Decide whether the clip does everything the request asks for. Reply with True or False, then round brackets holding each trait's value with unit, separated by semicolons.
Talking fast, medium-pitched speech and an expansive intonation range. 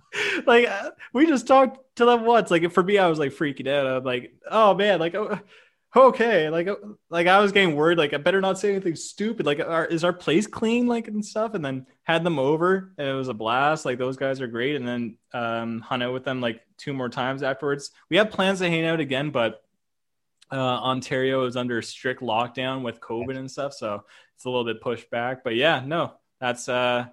True (225 wpm; 150 Hz; 7.5 semitones)